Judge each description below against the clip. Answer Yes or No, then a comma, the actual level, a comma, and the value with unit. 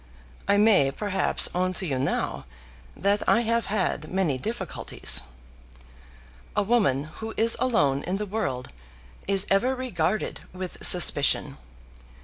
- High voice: Yes, high, 195 Hz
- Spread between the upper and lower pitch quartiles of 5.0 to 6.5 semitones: Yes, wide, 5.5 semitones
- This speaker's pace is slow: Yes, slow, 130 wpm